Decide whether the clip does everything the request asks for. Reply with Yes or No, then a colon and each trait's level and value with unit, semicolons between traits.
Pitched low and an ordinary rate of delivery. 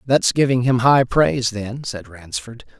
Yes: low, 120 Hz; average, 170 wpm